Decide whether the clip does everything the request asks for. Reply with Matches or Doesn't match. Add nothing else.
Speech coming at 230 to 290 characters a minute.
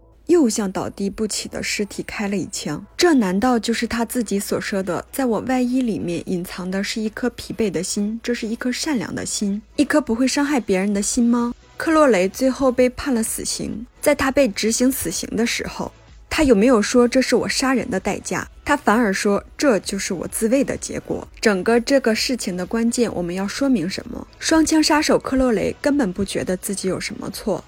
Doesn't match